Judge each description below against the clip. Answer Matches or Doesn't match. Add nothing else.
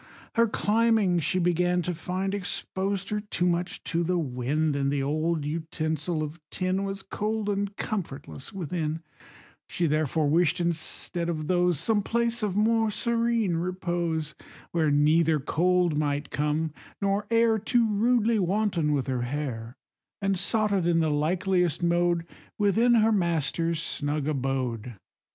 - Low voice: Doesn't match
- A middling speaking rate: Matches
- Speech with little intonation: Doesn't match